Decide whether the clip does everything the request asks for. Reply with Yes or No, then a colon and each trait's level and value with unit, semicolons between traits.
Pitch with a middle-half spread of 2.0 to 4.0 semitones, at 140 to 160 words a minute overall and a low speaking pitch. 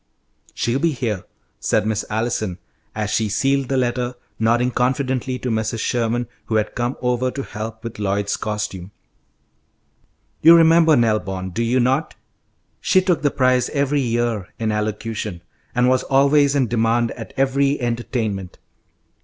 Yes: average, 3.4 semitones; average, 150 wpm; low, 120 Hz